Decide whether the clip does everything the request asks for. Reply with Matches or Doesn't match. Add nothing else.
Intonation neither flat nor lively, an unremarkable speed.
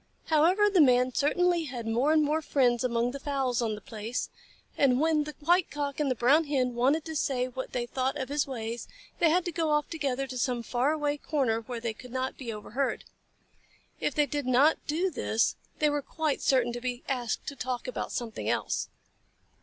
Doesn't match